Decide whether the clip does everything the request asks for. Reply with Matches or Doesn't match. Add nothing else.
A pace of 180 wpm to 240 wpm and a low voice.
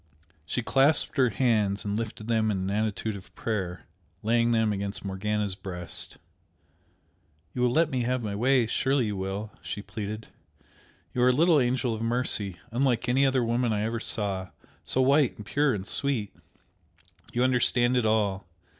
Doesn't match